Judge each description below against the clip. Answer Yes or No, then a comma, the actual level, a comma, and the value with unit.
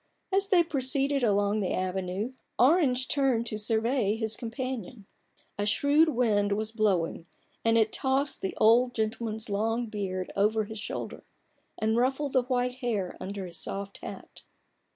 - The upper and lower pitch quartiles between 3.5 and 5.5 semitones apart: Yes, average, 4.0 semitones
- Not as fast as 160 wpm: Yes, average, 150 wpm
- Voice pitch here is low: No, high, 225 Hz